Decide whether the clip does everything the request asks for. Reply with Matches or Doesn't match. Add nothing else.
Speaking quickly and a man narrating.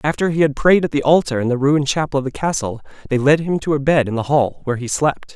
Matches